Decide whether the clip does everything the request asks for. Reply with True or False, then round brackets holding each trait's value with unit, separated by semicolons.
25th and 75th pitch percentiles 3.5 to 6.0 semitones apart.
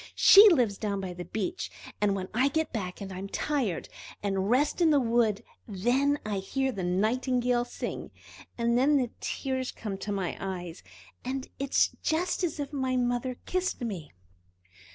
True (5.5 semitones)